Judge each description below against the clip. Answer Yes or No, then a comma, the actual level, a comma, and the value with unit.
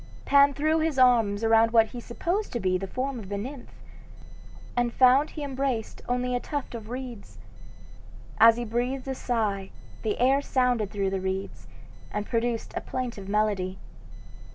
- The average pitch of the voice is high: Yes, high, 240 Hz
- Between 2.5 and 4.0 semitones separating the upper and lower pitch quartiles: Yes, average, 3.7 semitones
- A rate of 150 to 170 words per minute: Yes, average, 165 wpm